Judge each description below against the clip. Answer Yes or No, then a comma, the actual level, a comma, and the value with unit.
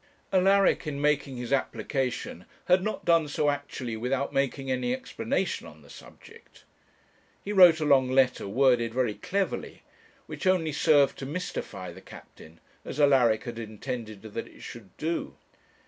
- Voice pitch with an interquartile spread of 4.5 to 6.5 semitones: Yes, average, 5.0 semitones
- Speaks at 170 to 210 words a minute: No, average, 150 wpm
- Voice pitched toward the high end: No, low, 135 Hz